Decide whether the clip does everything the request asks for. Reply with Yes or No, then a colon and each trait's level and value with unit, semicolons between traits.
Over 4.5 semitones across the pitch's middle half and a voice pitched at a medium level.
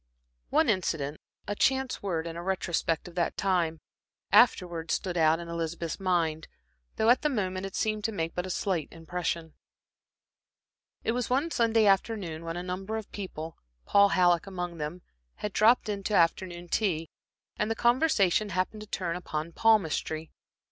No: average, 4.1 semitones; medium, 180 Hz